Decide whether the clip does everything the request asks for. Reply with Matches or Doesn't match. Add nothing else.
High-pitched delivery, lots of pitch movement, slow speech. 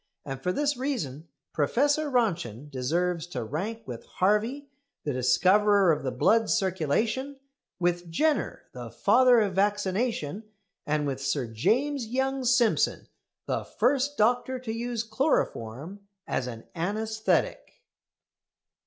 Matches